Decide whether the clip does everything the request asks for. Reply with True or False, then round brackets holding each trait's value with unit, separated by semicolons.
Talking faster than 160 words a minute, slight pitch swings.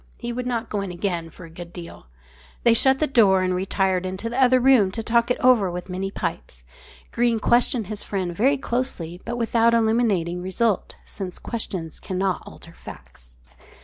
False (185 wpm; 4.7 semitones)